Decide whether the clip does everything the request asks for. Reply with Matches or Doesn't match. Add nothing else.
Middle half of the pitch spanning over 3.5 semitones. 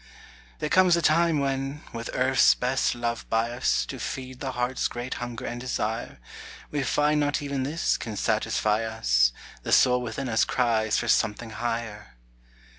Doesn't match